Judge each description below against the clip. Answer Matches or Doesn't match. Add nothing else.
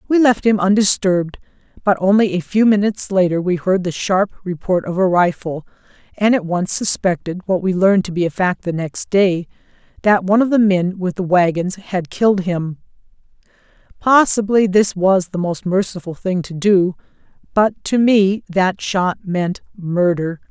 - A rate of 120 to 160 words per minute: Doesn't match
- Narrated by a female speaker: Matches